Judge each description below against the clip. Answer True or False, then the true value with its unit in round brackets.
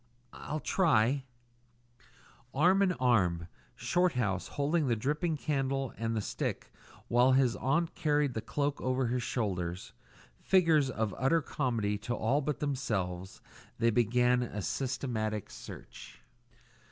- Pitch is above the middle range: False (125 Hz)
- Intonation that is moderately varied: True (4.7 semitones)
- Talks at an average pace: False (130 wpm)